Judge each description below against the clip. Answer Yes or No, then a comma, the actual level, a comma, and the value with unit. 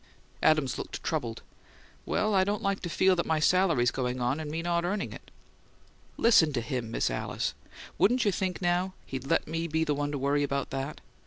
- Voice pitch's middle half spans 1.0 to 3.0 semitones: No, average, 5.2 semitones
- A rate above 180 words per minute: Yes, average, 200 wpm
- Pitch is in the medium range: Yes, medium, 155 Hz